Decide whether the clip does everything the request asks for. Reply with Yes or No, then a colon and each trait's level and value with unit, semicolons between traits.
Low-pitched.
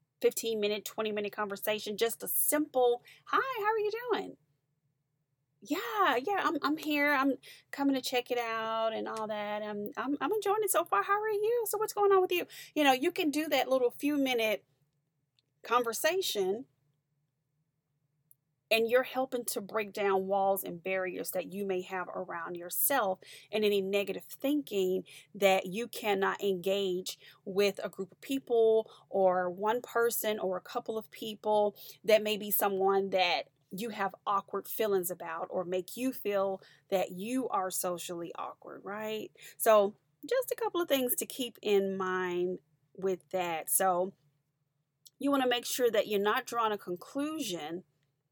No: high, 210 Hz